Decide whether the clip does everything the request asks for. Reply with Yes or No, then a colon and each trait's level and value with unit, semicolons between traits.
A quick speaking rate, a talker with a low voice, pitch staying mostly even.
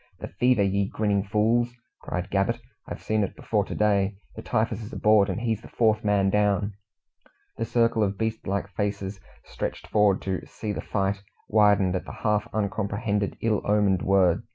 No: average, 175 wpm; low, 105 Hz; narrow, 1.7 semitones